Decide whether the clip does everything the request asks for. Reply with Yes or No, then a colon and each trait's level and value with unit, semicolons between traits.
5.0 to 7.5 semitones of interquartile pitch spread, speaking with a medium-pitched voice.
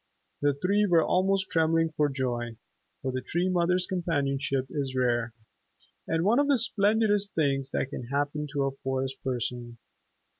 Yes: wide, 5.5 semitones; medium, 145 Hz